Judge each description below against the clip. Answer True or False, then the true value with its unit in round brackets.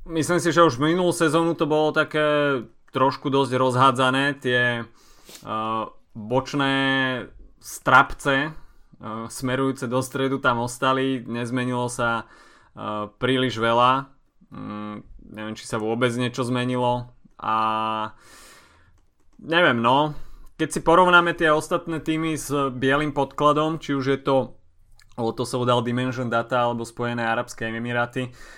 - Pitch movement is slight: False (3.5 semitones)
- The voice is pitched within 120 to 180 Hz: True (130 Hz)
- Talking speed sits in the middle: True (120 wpm)